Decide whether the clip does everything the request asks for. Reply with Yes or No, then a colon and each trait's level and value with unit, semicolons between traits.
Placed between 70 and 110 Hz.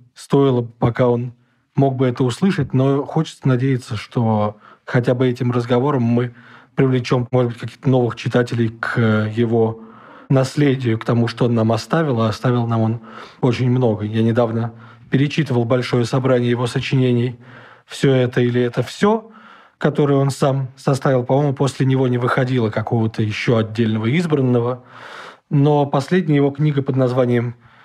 No: low, 125 Hz